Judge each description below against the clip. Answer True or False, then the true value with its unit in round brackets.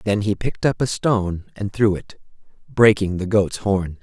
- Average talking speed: True (195 wpm)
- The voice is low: True (105 Hz)